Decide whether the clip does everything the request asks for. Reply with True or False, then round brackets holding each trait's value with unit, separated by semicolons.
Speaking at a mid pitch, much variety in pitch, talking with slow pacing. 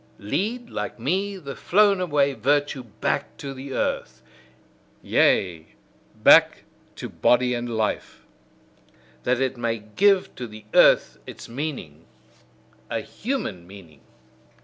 False (130 Hz; 7.5 semitones; 120 wpm)